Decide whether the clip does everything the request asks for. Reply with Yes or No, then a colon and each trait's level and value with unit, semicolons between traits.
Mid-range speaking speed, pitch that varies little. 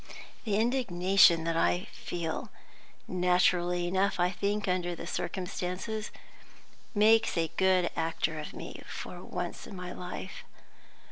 No: slow, 125 wpm; narrow, 2.2 semitones